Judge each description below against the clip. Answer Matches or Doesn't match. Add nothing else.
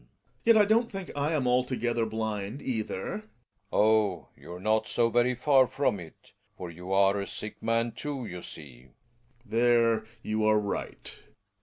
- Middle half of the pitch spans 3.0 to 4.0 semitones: Matches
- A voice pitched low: Matches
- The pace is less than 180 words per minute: Matches